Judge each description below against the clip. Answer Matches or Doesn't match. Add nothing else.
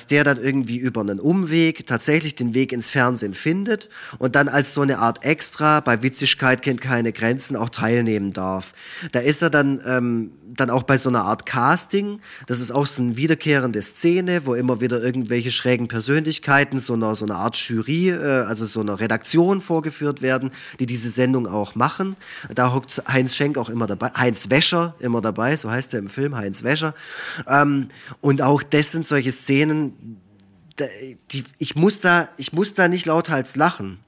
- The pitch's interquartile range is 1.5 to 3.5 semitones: Doesn't match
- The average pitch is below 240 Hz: Matches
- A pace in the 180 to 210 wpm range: Matches